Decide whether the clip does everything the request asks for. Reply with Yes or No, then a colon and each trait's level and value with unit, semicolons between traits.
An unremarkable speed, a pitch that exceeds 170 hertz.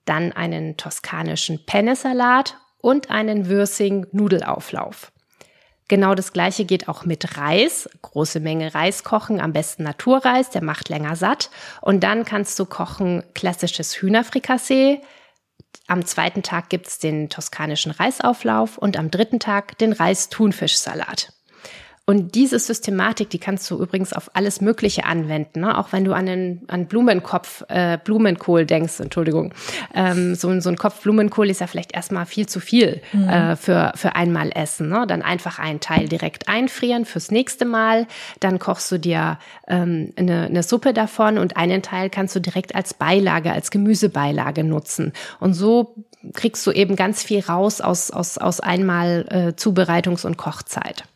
Yes: average, 155 wpm; high, 190 Hz